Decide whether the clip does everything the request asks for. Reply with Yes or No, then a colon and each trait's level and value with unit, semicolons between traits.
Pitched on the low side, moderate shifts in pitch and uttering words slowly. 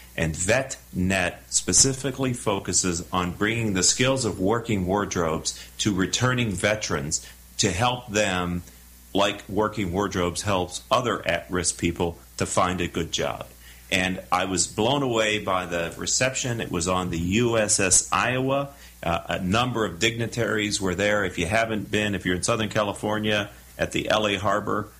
No: low, 100 Hz; average, 3.7 semitones; average, 155 wpm